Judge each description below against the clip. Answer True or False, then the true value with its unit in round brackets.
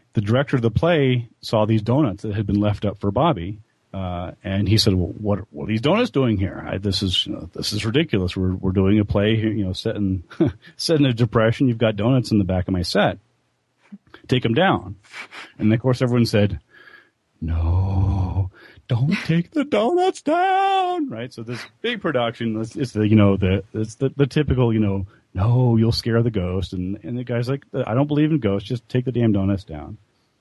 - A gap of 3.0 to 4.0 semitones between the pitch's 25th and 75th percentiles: False (4.8 semitones)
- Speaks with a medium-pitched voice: False (110 Hz)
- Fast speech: True (215 wpm)